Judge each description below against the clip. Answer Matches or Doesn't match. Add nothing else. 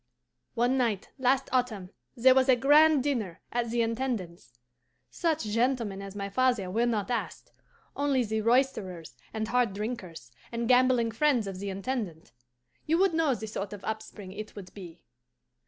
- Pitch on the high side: Matches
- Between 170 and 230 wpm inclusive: Doesn't match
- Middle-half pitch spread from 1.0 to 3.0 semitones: Doesn't match